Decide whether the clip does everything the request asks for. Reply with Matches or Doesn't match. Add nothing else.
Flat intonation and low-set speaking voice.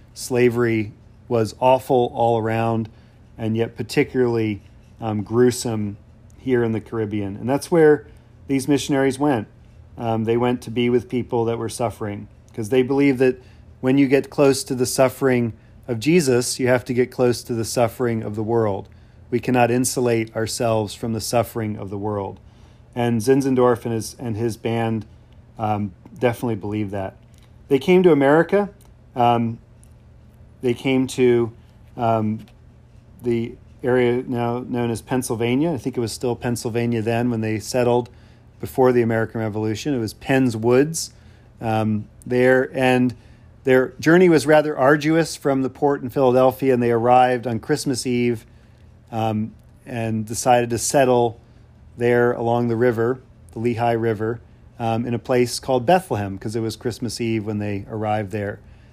Matches